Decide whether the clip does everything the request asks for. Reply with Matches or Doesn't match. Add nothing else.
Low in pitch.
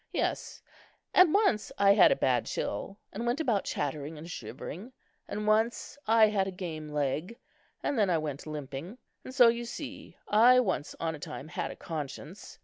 Doesn't match